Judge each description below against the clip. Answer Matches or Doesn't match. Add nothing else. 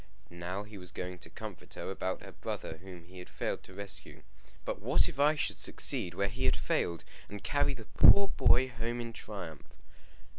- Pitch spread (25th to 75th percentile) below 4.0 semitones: Doesn't match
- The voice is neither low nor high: Doesn't match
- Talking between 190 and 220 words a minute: Matches